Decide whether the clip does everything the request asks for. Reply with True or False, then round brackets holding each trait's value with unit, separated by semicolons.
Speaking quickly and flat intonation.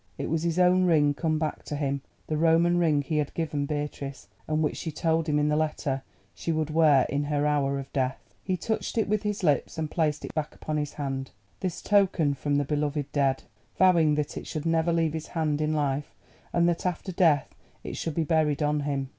True (220 wpm; 2.2 semitones)